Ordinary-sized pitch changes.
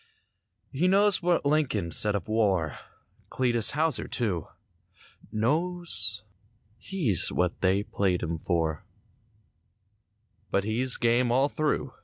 No: wide, 7.7 semitones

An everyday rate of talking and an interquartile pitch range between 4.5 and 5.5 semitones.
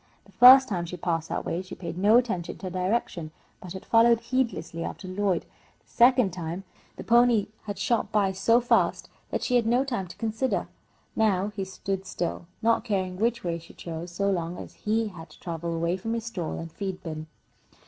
No: fast, 210 wpm; average, 4.8 semitones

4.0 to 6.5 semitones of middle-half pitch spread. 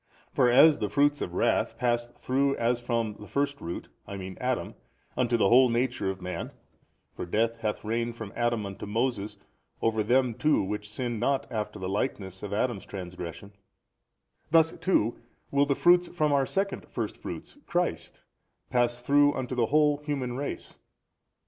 Yes: average, 4.9 semitones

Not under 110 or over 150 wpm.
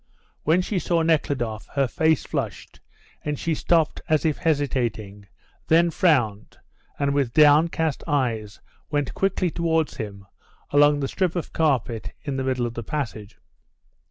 Yes: average, 145 wpm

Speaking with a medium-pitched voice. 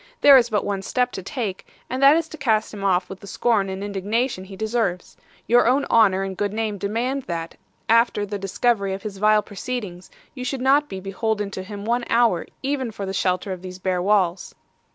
No: high, 205 Hz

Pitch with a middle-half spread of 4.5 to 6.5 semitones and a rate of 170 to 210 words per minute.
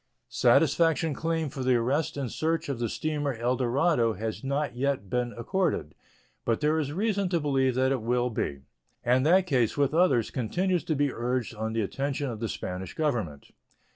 Yes: average, 4.8 semitones; average, 185 wpm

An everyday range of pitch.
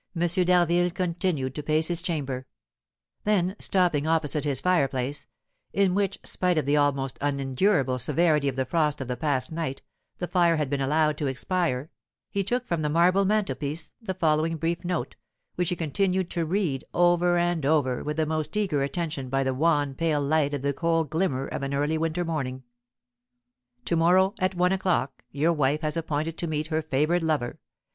Yes: average, 3.7 semitones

